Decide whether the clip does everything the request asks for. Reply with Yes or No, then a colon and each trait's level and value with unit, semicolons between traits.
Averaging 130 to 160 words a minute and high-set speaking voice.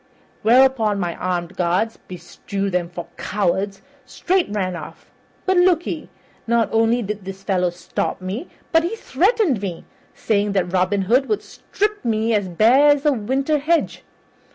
Yes: average, 155 wpm; high, 215 Hz